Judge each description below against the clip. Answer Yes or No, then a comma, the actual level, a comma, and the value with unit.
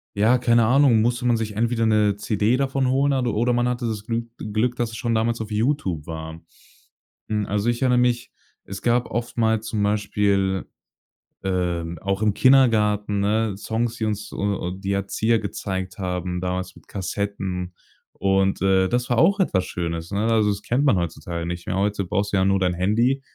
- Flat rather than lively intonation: No, average, 3.5 semitones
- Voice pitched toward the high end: No, low, 105 Hz